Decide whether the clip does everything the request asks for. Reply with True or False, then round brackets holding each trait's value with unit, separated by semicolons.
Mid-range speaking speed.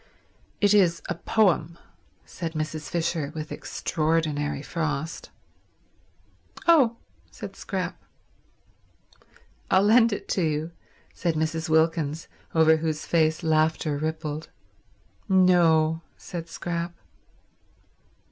False (95 wpm)